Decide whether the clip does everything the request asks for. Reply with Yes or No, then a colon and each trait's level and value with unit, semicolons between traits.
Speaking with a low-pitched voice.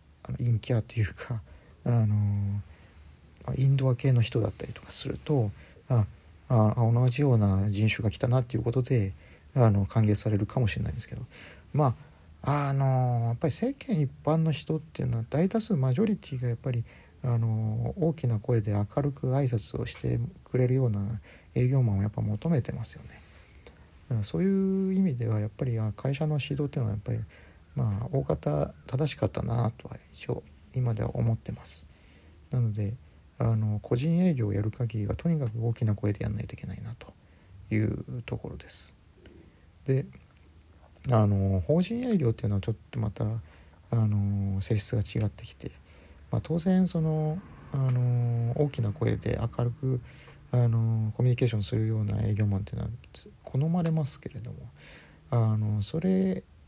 Yes: low, 115 Hz